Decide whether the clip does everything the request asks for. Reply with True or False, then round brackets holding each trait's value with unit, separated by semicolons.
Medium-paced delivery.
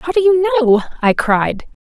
True (190 wpm)